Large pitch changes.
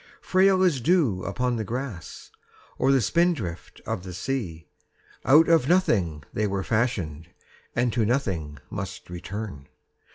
Yes: wide, 7.1 semitones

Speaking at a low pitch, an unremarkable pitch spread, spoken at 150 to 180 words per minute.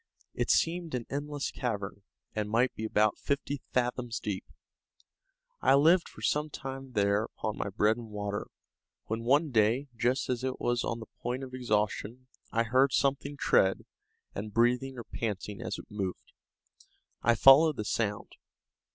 Yes: low, 120 Hz; average, 4.0 semitones; average, 160 wpm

